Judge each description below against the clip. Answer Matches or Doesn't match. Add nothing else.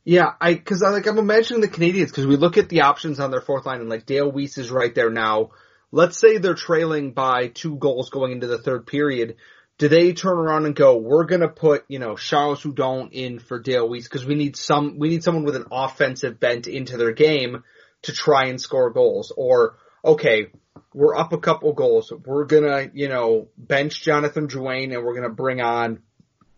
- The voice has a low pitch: Doesn't match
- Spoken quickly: Matches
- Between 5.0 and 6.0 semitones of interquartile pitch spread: Doesn't match